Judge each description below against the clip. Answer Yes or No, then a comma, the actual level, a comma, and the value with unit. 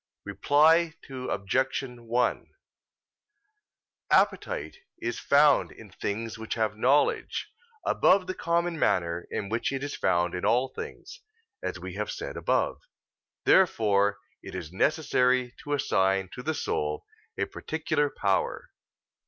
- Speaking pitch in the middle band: No, low, 125 Hz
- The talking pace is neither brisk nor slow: No, slow, 125 wpm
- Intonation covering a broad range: Yes, wide, 6.5 semitones